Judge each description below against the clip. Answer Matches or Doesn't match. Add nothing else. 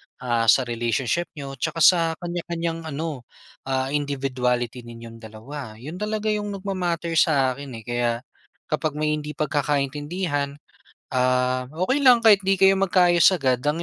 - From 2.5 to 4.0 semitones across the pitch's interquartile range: Doesn't match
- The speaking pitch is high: Doesn't match